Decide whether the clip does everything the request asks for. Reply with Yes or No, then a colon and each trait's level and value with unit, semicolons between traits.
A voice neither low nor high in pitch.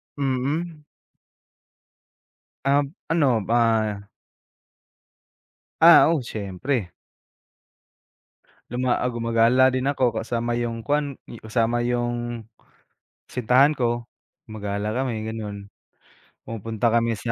No: low, 120 Hz